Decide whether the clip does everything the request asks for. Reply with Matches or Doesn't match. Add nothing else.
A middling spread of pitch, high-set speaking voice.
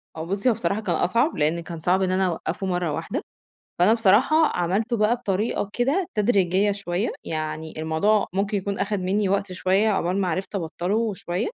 Matches